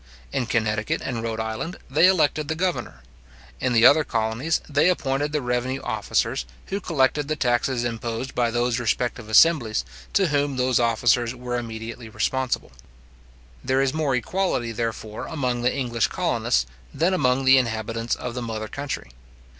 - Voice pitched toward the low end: Yes, low, 125 Hz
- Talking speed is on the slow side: No, average, 155 wpm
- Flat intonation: No, average, 3.7 semitones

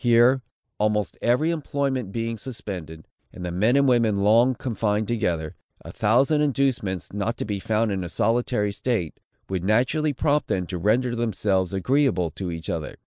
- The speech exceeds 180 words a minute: No, average, 165 wpm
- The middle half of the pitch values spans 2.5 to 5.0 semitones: Yes, average, 4.7 semitones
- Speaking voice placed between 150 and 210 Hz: No, low, 110 Hz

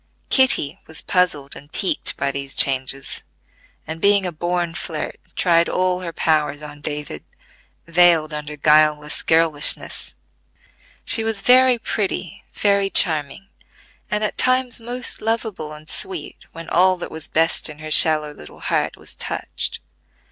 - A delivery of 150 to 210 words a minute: No, average, 140 wpm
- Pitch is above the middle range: No, medium, 165 Hz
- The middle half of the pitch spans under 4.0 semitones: No, average, 4.5 semitones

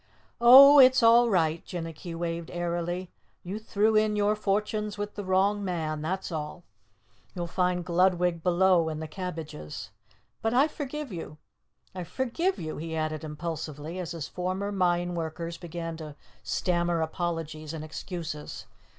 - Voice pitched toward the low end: No, medium, 175 Hz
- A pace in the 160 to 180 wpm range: No, average, 145 wpm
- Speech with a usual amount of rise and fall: Yes, average, 3.9 semitones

